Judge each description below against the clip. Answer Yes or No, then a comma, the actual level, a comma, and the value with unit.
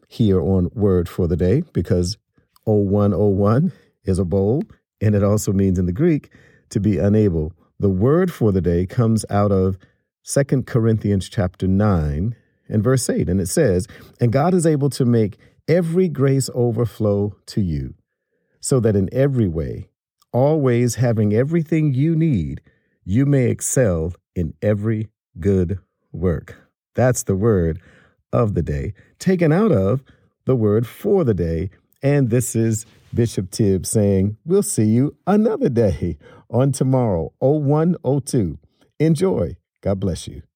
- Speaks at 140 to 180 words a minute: Yes, average, 145 wpm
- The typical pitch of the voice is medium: No, low, 110 Hz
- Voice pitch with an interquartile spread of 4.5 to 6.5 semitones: Yes, wide, 5.4 semitones